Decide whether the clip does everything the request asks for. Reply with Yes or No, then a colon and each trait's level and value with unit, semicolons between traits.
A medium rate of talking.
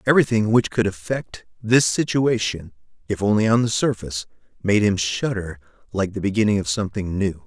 Yes: average, 160 wpm